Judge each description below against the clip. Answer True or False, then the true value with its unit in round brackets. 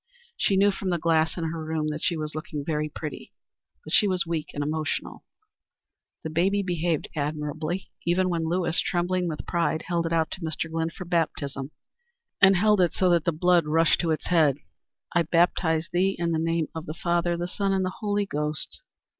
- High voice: False (170 Hz)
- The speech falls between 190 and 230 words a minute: True (200 wpm)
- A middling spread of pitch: False (2.2 semitones)